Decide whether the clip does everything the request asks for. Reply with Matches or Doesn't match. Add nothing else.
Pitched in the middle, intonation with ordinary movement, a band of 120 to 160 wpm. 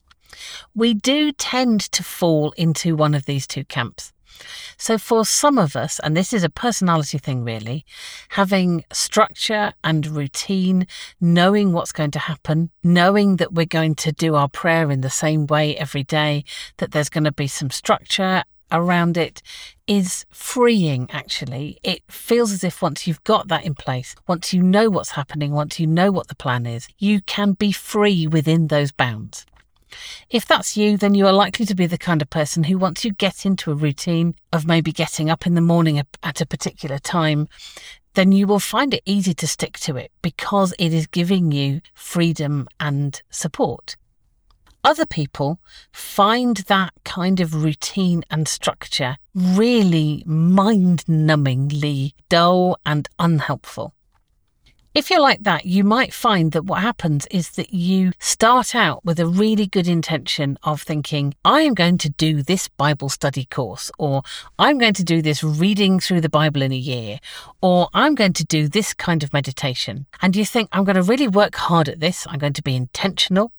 Doesn't match